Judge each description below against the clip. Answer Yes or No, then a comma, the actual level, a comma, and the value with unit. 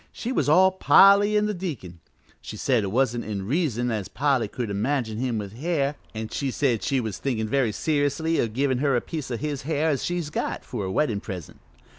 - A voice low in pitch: Yes, low, 130 Hz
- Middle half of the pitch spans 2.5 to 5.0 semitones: No, wide, 5.5 semitones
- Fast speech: Yes, fast, 215 wpm